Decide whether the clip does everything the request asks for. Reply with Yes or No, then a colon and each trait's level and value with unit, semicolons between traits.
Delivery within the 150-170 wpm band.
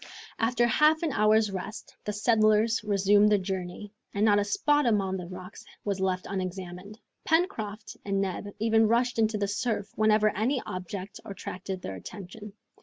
Yes: average, 160 wpm